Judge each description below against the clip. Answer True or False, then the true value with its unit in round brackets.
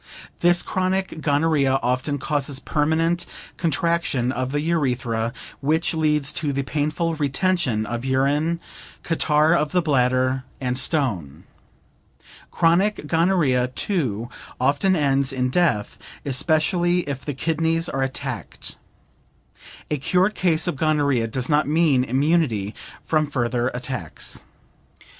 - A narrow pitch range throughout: False (4.2 semitones)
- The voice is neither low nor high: True (145 Hz)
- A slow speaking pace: True (115 wpm)